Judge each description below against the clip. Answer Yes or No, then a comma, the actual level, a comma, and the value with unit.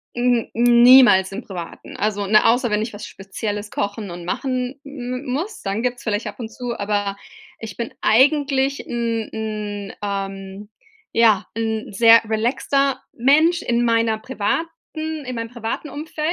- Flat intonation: No, average, 3.5 semitones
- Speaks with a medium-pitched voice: No, high, 230 Hz